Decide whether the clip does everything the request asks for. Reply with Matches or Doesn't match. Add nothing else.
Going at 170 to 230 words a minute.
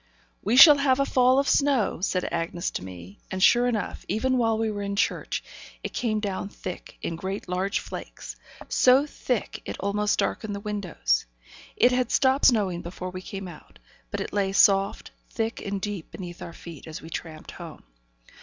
Matches